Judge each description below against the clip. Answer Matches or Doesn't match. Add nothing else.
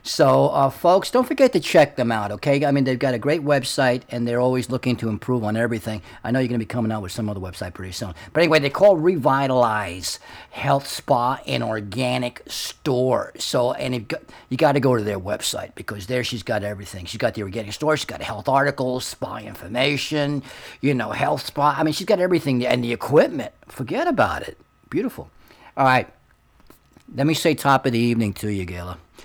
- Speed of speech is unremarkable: Doesn't match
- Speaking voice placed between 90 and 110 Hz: Doesn't match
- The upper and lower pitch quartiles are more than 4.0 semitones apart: Matches